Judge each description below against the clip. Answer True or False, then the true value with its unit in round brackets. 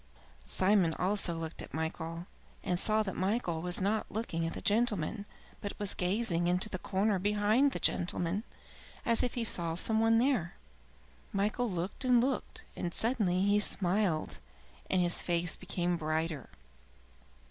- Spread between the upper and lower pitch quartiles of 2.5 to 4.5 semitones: True (4.0 semitones)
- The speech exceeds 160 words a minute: False (150 wpm)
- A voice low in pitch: False (190 Hz)